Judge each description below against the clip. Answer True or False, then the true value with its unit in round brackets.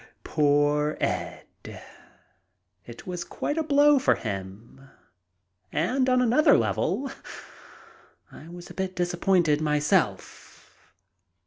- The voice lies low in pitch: False (175 Hz)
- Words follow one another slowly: True (100 wpm)